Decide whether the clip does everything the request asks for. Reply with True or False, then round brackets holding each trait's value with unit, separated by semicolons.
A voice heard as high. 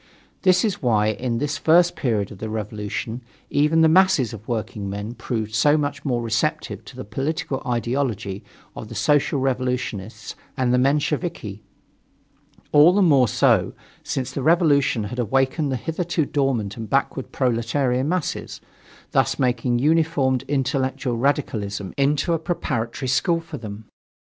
False (130 Hz)